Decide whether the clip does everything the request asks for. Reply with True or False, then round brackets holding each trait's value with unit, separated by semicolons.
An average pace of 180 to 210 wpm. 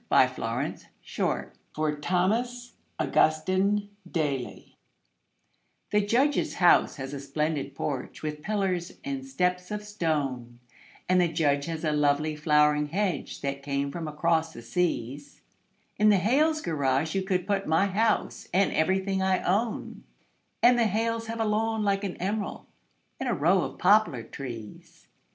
False (150 wpm)